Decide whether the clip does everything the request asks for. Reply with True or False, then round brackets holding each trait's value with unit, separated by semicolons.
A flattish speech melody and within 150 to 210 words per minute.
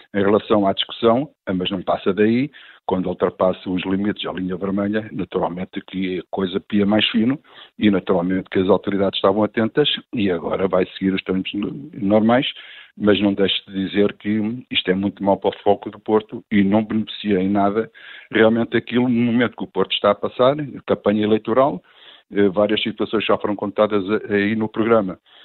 True (2.1 semitones; 180 wpm)